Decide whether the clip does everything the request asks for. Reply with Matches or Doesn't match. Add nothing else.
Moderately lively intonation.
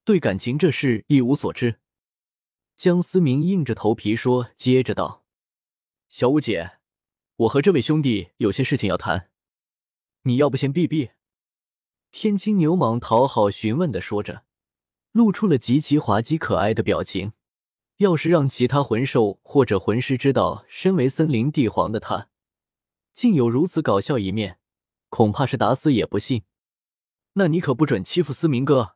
Doesn't match